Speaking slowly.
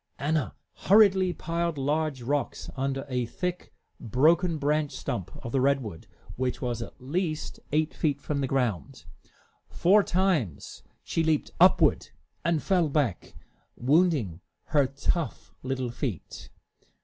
Yes: slow, 125 wpm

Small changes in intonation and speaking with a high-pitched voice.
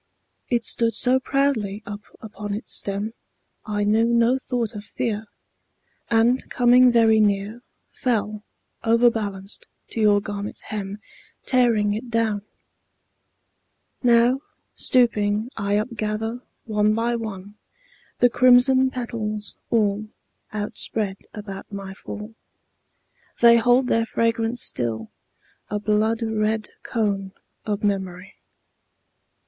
Yes: narrow, 2.3 semitones; high, 220 Hz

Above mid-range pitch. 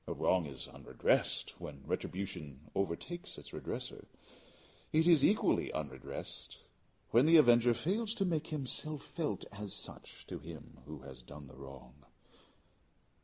No: low, 100 Hz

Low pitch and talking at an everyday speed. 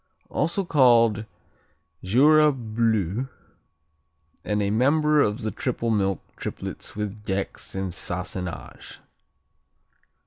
No: low, 110 Hz; slow, 95 wpm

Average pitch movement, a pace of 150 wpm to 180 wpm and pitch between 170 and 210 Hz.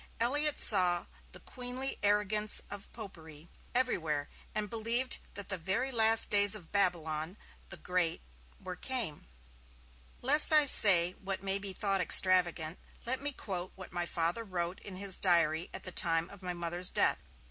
Yes: average, 4.1 semitones; average, 160 wpm; high, 190 Hz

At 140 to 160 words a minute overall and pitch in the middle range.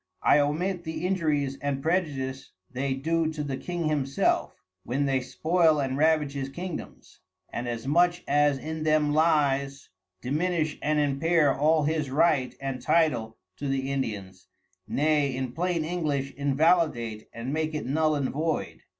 Yes: average, 150 wpm; medium, 145 Hz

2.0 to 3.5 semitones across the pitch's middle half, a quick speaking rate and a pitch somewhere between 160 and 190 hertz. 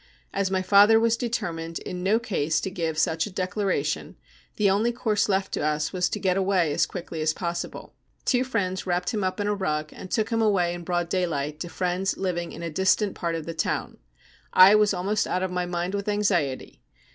Yes: average, 3.2 semitones; fast, 215 wpm; medium, 185 Hz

